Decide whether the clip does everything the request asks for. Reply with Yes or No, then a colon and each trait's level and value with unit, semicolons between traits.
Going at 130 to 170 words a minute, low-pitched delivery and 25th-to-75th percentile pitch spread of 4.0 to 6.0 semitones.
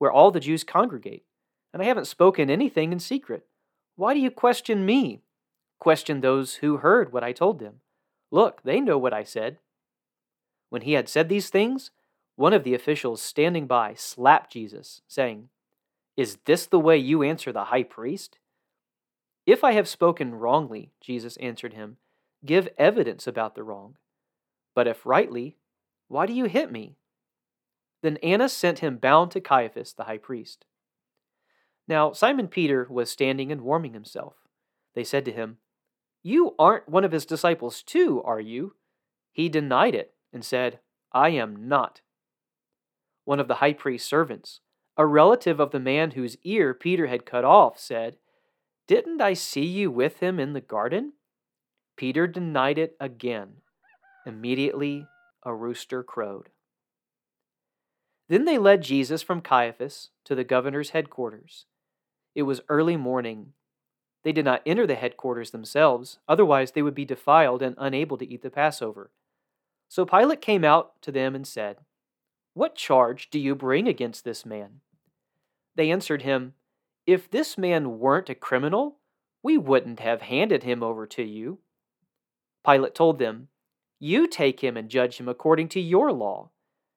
No: average, 155 wpm; medium, 145 Hz; wide, 5.6 semitones